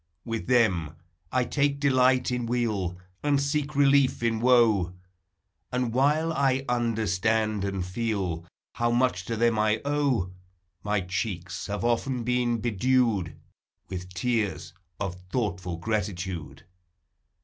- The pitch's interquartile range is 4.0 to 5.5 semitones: Yes, average, 4.8 semitones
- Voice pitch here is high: No, low, 115 Hz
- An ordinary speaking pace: No, slow, 120 wpm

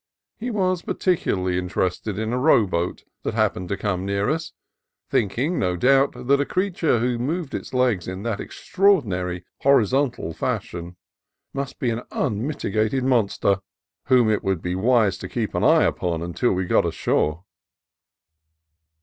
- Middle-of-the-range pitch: No, low, 110 Hz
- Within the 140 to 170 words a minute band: Yes, average, 155 wpm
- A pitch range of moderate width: No, wide, 6.8 semitones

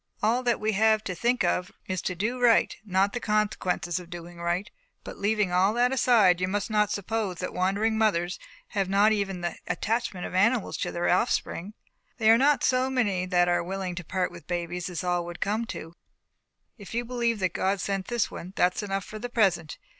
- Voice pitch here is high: Yes, high, 195 Hz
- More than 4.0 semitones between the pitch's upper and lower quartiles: No, average, 3.6 semitones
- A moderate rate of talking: No, fast, 215 wpm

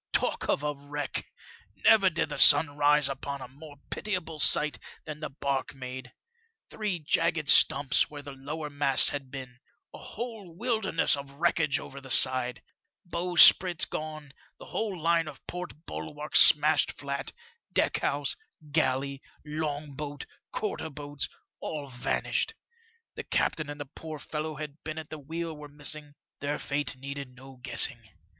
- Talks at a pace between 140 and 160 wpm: Yes, average, 155 wpm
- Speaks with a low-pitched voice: No, medium, 145 Hz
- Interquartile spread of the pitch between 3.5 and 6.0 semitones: No, narrow, 2.4 semitones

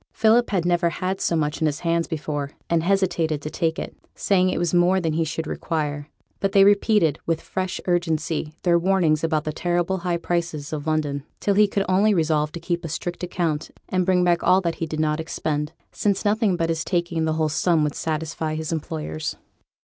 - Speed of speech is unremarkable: No, fast, 210 wpm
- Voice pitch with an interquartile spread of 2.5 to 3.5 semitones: Yes, average, 2.8 semitones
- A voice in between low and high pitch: Yes, medium, 165 Hz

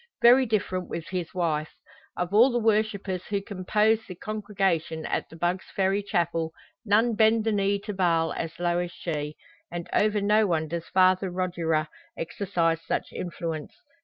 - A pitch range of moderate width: Yes, average, 3.7 semitones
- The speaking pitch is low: No, medium, 185 Hz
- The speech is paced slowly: No, average, 160 wpm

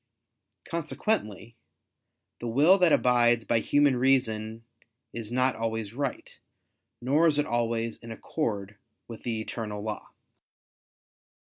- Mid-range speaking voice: No, low, 120 Hz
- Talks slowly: Yes, slow, 115 wpm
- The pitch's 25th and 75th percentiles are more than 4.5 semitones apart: No, average, 3.3 semitones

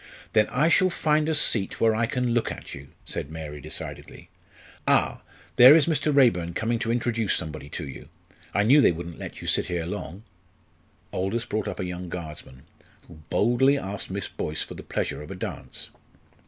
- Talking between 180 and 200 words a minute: Yes, average, 190 wpm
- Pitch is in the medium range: No, low, 105 Hz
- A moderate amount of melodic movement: No, wide, 6.5 semitones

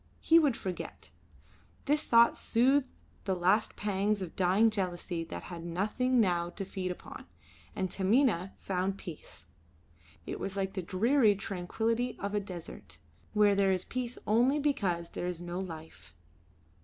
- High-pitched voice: Yes, high, 195 Hz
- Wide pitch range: No, average, 4.2 semitones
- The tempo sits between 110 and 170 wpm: Yes, average, 150 wpm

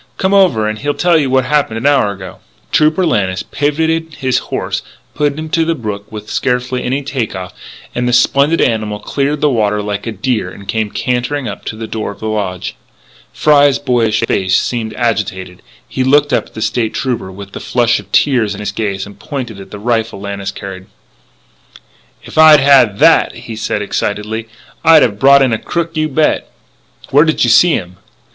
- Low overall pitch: Yes, low, 120 Hz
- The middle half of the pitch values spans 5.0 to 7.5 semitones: Yes, wide, 5.6 semitones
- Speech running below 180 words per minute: No, average, 200 wpm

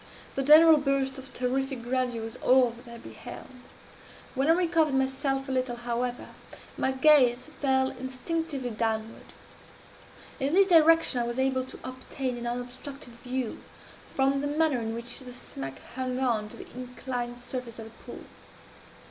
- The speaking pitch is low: No, very high, 260 Hz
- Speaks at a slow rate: No, average, 155 wpm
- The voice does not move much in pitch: Yes, narrow, 2.1 semitones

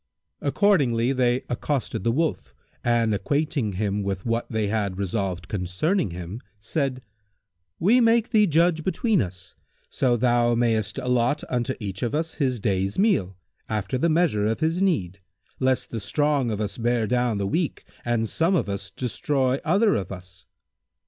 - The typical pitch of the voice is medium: No, low, 120 Hz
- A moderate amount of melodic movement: No, wide, 6.5 semitones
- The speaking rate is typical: Yes, average, 160 wpm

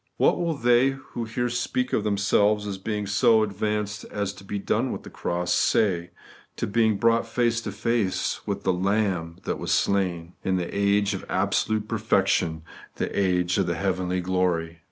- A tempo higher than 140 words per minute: Yes, average, 185 wpm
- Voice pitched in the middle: No, low, 100 Hz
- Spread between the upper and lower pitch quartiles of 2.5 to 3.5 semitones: Yes, average, 3.2 semitones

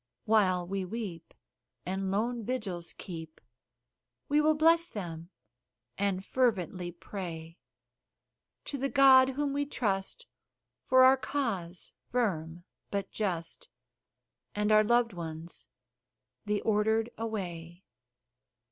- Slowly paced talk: Yes, slow, 105 wpm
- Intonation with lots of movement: Yes, wide, 5.9 semitones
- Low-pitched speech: No, high, 205 Hz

